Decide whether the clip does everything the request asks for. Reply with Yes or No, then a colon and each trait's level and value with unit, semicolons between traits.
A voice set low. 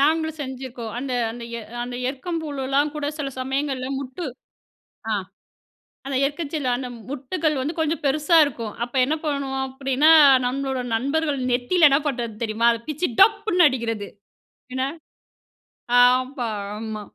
No: very high, 270 Hz